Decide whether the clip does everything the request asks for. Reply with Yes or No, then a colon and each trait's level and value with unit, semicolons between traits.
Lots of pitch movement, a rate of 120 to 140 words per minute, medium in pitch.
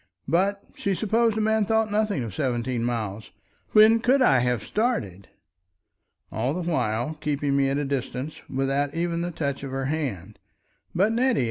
No: wide, 8.5 semitones; average, 165 wpm; medium, 145 Hz